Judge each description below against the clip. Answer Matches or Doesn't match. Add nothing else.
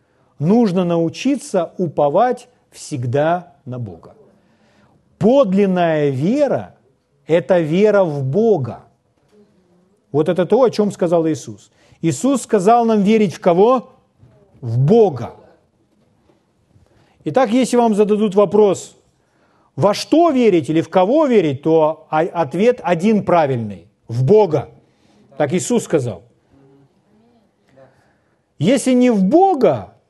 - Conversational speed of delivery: Doesn't match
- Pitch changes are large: Matches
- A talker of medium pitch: Matches